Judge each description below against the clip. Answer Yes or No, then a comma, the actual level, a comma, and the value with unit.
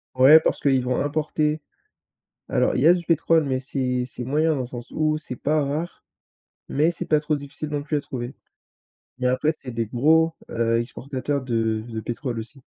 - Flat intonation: No, average, 3.5 semitones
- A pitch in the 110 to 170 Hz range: Yes, medium, 140 Hz